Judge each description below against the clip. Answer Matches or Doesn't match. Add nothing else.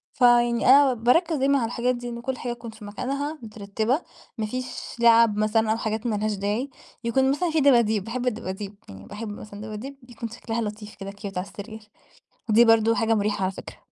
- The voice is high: Matches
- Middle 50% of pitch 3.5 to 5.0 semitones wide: Doesn't match